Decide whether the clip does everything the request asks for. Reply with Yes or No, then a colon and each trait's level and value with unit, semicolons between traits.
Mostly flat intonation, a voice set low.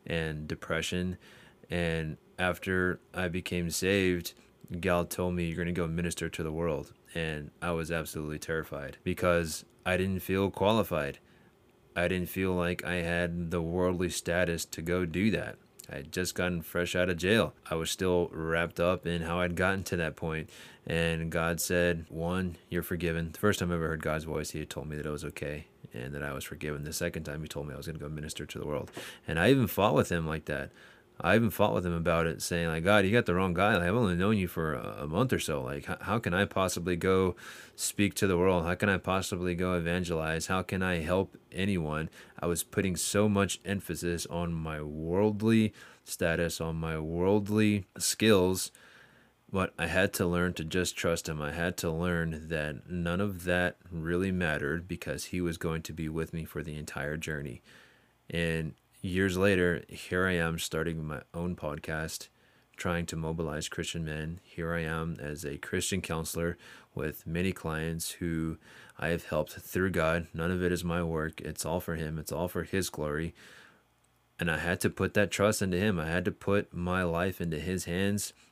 Yes: narrow, 2.1 semitones; very low, 85 Hz